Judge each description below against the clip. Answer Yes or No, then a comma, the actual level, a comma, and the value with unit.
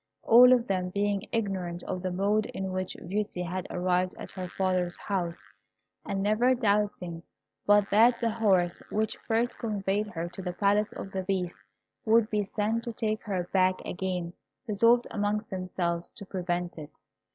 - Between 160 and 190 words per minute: Yes, average, 165 wpm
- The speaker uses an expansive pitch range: No, average, 2.9 semitones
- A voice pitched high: Yes, high, 195 Hz